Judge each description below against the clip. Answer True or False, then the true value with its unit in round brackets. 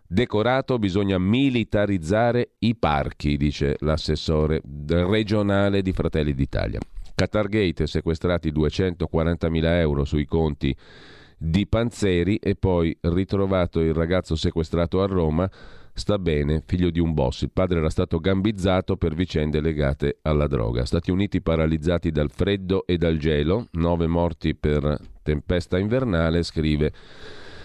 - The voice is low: True (85 Hz)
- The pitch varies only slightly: False (3.7 semitones)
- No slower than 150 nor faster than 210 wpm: False (125 wpm)